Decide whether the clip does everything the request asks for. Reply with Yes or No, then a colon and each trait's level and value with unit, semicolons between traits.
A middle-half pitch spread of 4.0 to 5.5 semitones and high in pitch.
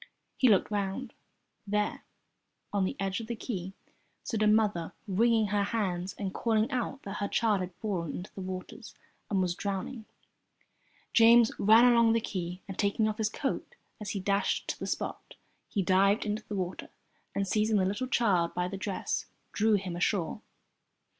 No: average, 2.7 semitones; high, 205 Hz